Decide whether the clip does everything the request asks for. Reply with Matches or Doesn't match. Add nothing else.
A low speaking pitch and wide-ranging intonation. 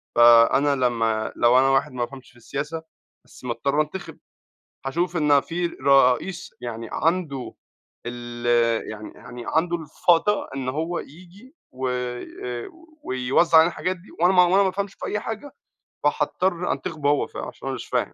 Doesn't match